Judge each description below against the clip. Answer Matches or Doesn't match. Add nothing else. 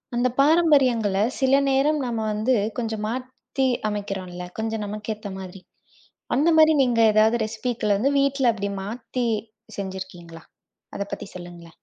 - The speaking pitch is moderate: Doesn't match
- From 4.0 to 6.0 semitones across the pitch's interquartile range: Matches